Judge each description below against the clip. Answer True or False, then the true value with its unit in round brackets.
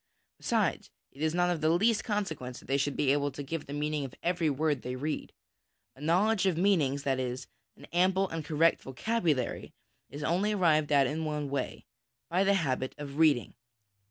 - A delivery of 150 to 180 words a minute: False (190 wpm)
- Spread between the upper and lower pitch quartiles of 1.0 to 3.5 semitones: False (4.1 semitones)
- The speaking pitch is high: False (155 Hz)